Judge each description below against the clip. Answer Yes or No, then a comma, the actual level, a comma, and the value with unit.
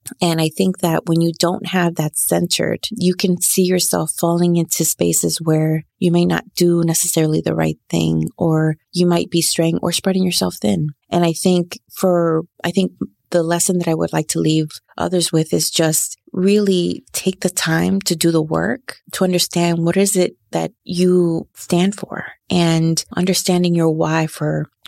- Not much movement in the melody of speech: Yes, narrow, 2.3 semitones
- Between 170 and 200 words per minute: Yes, average, 180 wpm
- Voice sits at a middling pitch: Yes, medium, 170 Hz